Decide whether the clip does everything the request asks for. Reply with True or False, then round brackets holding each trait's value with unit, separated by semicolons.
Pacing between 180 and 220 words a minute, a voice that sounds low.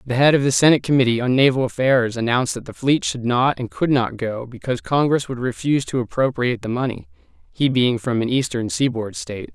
True (205 wpm; 125 Hz)